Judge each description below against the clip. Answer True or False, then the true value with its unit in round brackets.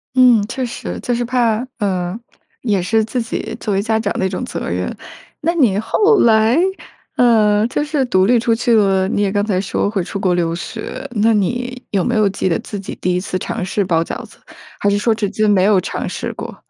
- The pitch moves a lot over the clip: False (3.5 semitones)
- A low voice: False (215 Hz)